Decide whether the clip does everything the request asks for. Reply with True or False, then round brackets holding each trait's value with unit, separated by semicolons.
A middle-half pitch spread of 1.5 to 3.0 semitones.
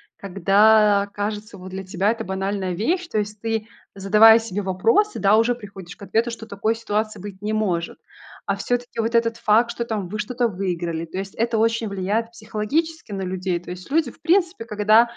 True (2.7 semitones)